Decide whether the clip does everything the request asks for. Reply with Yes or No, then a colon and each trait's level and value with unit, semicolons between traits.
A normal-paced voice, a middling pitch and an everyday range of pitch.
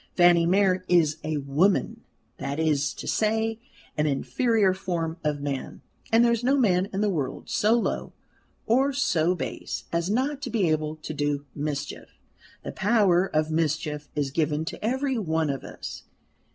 No: average, 165 wpm; medium, 170 Hz; wide, 5.9 semitones